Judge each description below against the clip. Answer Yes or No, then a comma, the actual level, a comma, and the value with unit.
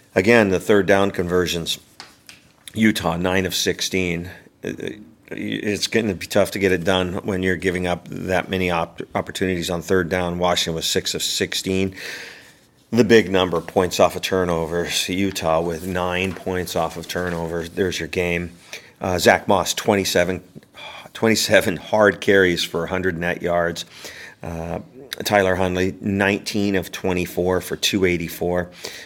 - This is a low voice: Yes, very low, 90 Hz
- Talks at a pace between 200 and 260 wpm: No, average, 145 wpm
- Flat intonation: Yes, narrow, 1.7 semitones